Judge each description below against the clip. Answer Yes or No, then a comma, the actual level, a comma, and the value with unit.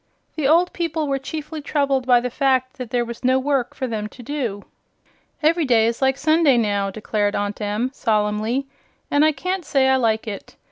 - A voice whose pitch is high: Yes, very high, 260 Hz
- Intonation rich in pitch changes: No, average, 4.5 semitones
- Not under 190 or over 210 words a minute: Yes, average, 195 wpm